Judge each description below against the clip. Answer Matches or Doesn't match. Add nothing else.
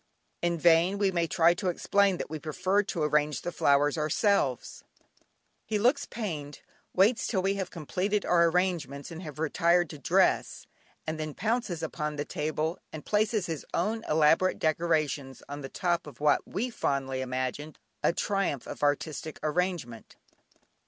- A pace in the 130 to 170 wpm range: Matches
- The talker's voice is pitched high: Doesn't match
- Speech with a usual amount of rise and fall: Matches